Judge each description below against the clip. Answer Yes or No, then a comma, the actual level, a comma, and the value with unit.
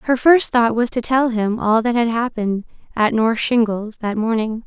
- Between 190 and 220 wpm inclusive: Yes, fast, 205 wpm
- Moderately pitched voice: No, high, 230 Hz